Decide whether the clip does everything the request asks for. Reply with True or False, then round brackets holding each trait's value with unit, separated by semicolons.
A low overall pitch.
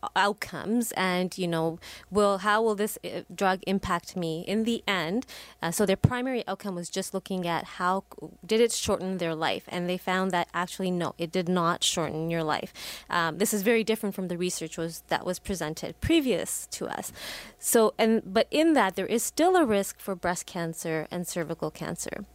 False (185 Hz)